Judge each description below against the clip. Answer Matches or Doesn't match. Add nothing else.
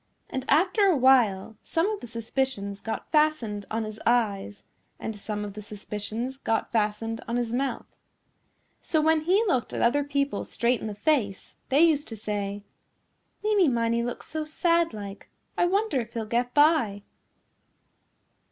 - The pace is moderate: Matches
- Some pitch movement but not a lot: Doesn't match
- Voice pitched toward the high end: Matches